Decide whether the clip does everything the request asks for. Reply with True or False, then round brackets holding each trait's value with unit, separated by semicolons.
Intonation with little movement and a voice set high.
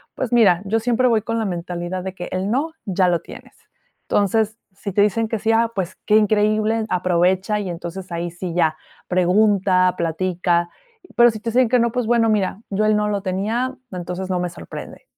False (3.7 semitones; 200 Hz)